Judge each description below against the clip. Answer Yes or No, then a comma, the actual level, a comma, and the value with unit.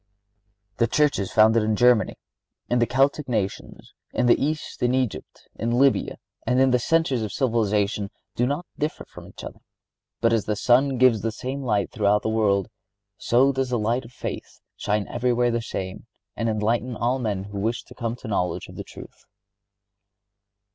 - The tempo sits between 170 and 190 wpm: Yes, average, 180 wpm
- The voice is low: Yes, low, 120 Hz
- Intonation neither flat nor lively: Yes, average, 3.1 semitones